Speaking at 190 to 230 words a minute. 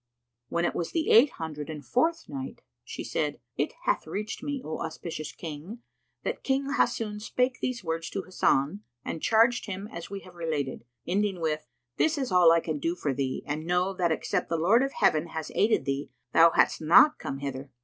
Yes: average, 200 wpm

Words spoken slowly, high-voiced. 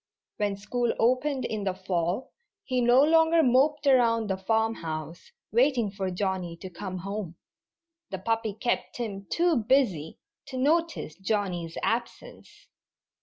Yes: slow, 130 wpm; high, 220 Hz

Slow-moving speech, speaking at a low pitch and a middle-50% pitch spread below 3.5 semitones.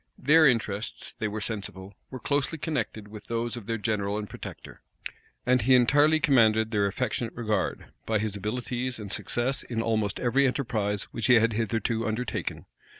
No: average, 165 wpm; low, 115 Hz; average, 3.0 semitones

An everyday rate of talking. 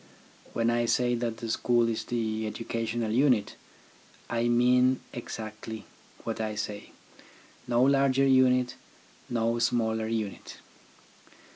No: slow, 115 wpm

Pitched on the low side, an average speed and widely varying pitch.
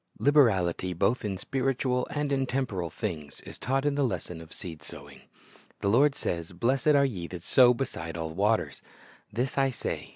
Yes: low, 115 Hz; average, 175 wpm; wide, 7.4 semitones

